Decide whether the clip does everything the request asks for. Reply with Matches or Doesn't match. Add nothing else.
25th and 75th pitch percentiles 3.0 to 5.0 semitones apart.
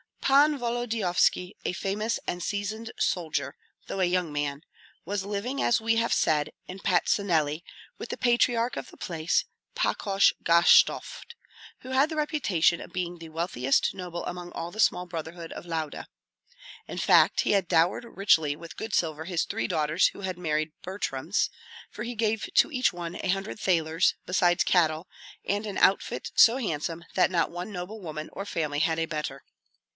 Matches